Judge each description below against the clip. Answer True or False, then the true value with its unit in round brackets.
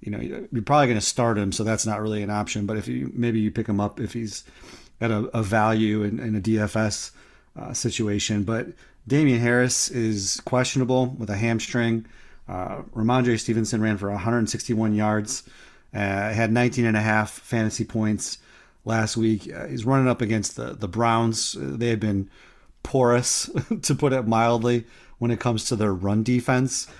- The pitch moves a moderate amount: False (2.1 semitones)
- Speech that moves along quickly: False (180 wpm)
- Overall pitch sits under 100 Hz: False (115 Hz)